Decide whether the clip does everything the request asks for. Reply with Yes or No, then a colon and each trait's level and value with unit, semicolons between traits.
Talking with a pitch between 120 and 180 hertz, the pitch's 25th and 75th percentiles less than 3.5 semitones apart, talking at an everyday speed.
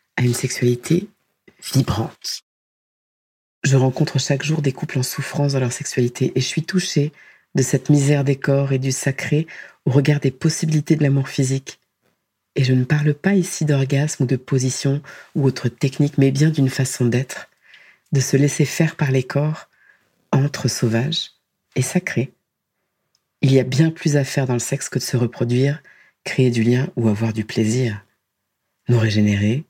Yes: low, 135 Hz; average, 2.8 semitones; average, 175 wpm